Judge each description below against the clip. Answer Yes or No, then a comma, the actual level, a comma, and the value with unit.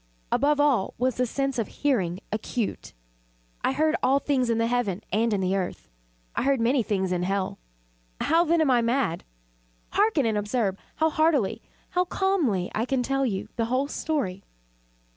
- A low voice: No, high, 245 Hz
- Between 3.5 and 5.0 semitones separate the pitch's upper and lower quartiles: No, wide, 5.5 semitones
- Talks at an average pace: Yes, average, 175 wpm